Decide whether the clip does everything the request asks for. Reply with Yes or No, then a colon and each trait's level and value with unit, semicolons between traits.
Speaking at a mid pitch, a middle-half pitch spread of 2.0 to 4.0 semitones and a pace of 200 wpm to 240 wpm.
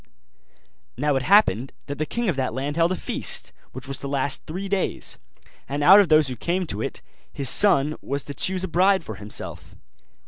No: medium, 145 Hz; wide, 5.5 semitones; fast, 205 wpm